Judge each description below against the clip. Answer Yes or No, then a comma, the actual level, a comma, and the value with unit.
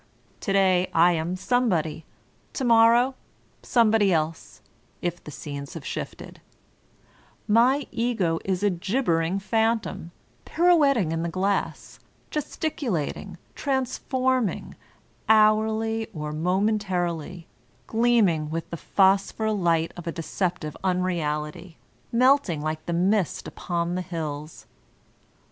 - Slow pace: Yes, slow, 110 wpm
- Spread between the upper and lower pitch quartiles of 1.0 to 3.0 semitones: No, average, 5.2 semitones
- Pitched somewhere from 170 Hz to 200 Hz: Yes, medium, 185 Hz